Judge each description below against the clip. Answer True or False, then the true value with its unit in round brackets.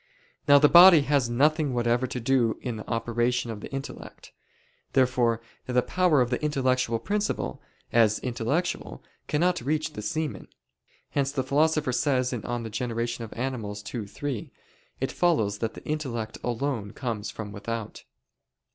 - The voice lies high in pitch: False (125 Hz)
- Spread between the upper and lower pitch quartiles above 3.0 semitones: True (3.8 semitones)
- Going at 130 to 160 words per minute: True (145 wpm)